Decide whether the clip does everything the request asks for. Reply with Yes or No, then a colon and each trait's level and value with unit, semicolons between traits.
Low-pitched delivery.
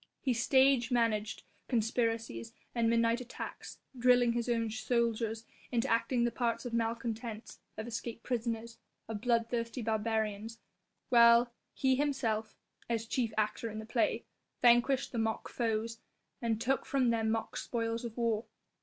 No: high, 230 Hz